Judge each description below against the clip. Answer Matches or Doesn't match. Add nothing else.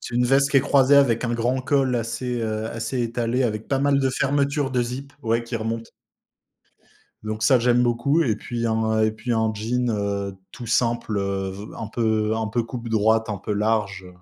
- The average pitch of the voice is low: Matches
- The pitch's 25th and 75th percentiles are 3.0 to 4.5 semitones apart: Doesn't match